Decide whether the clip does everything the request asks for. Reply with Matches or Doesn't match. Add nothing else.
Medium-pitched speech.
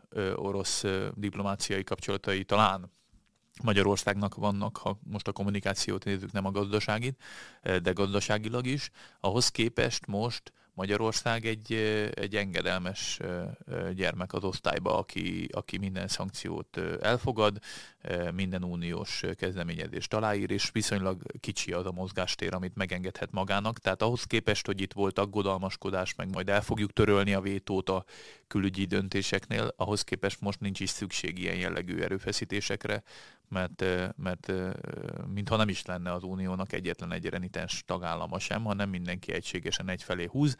Doesn't match